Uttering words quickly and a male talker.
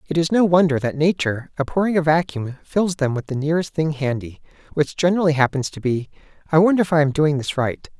Yes: fast, 220 wpm; male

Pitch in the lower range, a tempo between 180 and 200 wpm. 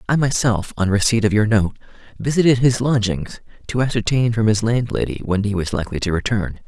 Yes: low, 110 Hz; average, 190 wpm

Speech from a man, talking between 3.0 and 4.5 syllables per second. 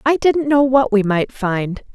No: female; 4.0 syllables/s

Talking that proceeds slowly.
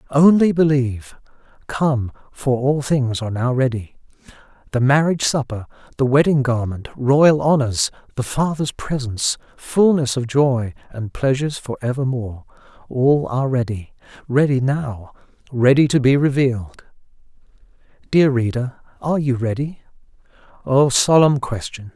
Yes: slow, 110 wpm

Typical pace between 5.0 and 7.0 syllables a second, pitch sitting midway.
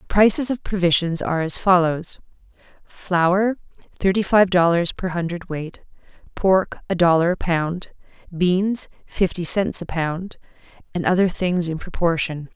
No: 4.4 syllables/s; medium, 180 Hz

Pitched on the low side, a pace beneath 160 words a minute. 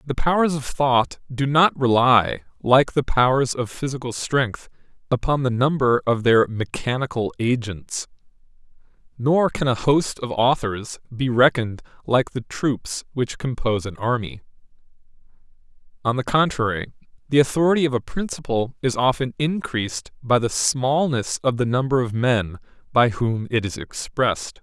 Yes: low, 125 Hz; average, 145 wpm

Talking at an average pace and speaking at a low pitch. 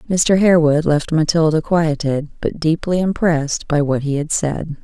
No: average, 160 wpm; medium, 160 Hz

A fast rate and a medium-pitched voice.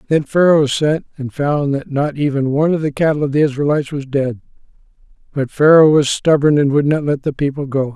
Yes: fast, 210 wpm; medium, 145 Hz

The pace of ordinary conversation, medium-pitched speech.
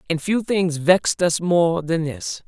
Yes: average, 195 wpm; medium, 170 Hz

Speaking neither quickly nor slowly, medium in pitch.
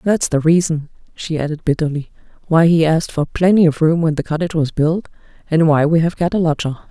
No: fast, 215 wpm; medium, 160 Hz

